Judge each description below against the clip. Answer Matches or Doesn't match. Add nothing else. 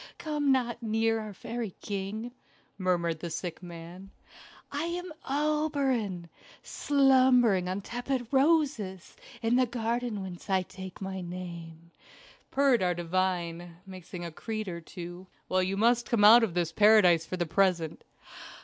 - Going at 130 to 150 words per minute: Matches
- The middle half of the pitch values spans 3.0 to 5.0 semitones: Doesn't match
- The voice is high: Matches